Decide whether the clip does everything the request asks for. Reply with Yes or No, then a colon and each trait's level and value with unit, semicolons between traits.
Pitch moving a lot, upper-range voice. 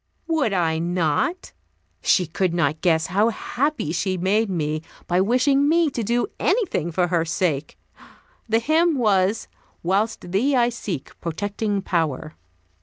Yes: wide, 6.0 semitones; high, 195 Hz